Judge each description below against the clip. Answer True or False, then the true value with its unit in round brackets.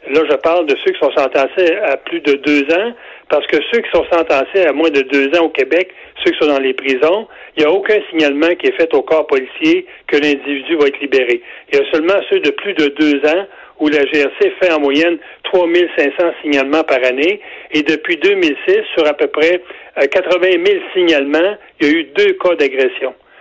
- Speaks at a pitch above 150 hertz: True (190 Hz)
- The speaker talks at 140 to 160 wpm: False (220 wpm)